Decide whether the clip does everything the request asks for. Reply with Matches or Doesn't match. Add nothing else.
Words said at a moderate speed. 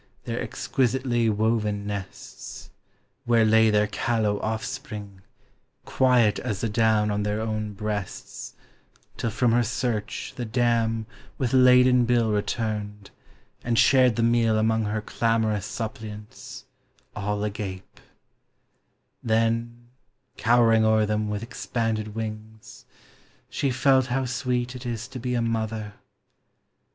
Doesn't match